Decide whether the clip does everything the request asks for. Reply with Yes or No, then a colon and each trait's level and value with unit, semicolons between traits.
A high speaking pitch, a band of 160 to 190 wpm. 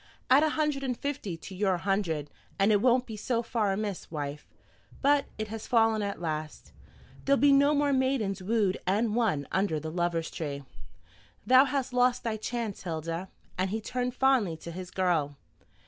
Yes: high, 210 Hz; average, 180 wpm